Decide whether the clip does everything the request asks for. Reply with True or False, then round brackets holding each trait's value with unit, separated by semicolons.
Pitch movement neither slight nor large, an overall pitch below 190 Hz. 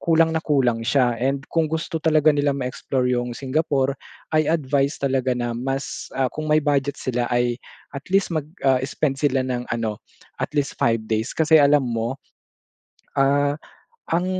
True (3.3 semitones; 135 Hz)